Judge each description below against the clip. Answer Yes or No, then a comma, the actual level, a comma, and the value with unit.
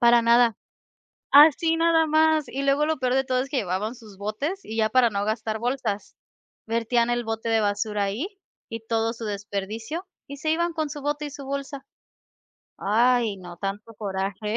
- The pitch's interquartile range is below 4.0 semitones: No, average, 4.8 semitones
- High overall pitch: Yes, high, 235 Hz